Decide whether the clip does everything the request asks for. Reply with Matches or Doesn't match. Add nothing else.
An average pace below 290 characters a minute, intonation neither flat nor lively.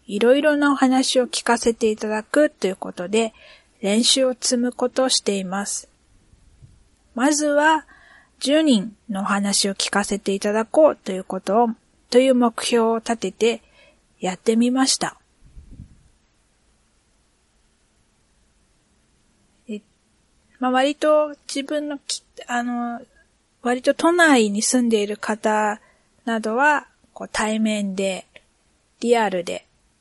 Matches